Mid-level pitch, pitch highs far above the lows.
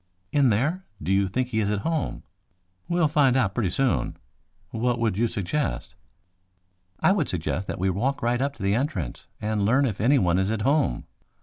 No: low, 115 Hz; wide, 5.8 semitones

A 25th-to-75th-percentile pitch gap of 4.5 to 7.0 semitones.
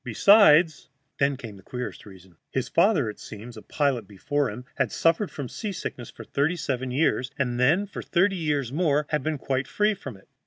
Yes: average, 5.1 semitones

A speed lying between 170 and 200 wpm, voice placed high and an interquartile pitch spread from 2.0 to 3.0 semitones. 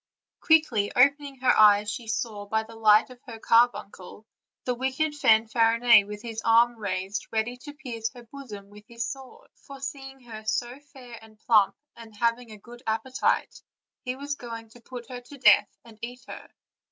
Yes: average, 175 wpm; high, 235 Hz; narrow, 2.6 semitones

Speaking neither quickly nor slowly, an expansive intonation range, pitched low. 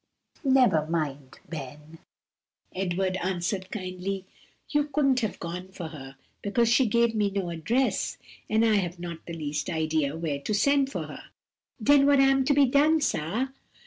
No: average, 160 wpm; wide, 7.8 semitones; high, 190 Hz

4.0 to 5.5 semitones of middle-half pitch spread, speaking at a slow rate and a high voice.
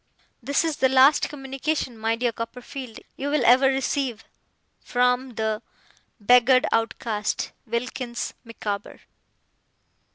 No: average, 2.8 semitones; slow, 105 wpm; very high, 250 Hz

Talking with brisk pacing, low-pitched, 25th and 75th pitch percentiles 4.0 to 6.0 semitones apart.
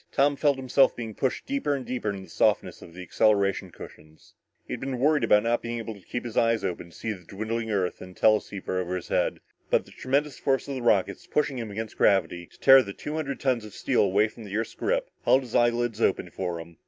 Yes: fast, 245 wpm; low, 115 Hz; average, 5.1 semitones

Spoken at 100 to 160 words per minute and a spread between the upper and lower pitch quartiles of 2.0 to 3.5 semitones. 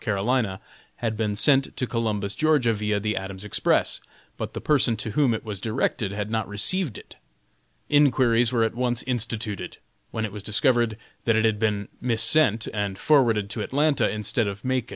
No: average, 175 wpm; average, 3.2 semitones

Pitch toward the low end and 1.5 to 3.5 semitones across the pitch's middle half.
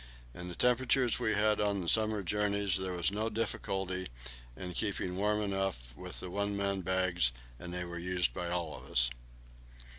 Yes: very low, 95 Hz; average, 2.7 semitones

